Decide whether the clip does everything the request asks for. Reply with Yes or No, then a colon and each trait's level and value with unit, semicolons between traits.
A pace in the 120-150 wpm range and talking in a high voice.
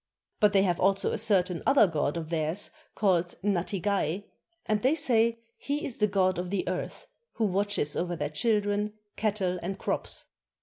No: average, 170 wpm; high, 195 Hz